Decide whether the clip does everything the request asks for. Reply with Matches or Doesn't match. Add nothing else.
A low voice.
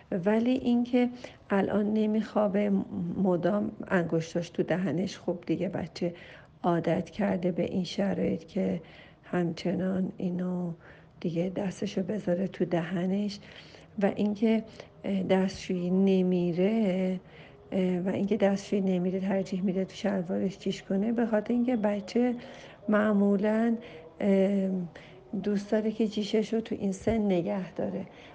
Doesn't match